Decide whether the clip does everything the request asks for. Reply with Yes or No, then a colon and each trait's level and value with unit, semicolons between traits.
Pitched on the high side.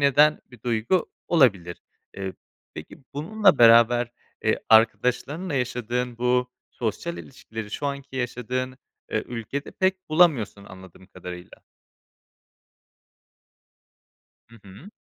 No: low, 125 Hz